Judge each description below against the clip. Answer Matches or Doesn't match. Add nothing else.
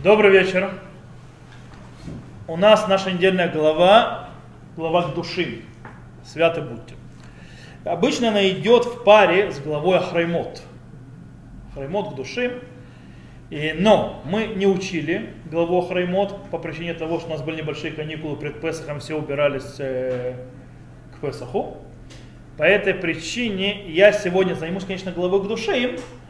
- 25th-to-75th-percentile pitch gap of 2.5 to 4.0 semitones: Doesn't match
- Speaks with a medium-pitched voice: Matches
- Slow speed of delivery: Doesn't match